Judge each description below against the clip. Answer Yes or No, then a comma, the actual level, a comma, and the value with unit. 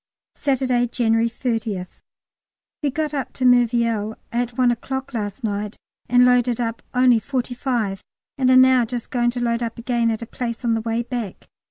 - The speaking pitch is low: No, high, 240 Hz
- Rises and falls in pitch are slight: Yes, narrow, 1.8 semitones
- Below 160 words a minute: No, average, 180 wpm